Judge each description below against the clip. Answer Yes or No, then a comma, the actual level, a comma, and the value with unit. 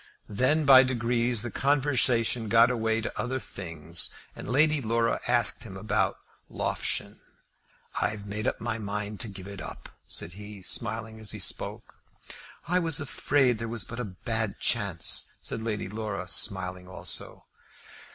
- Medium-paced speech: Yes, average, 150 wpm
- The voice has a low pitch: Yes, low, 110 Hz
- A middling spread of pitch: Yes, average, 3.4 semitones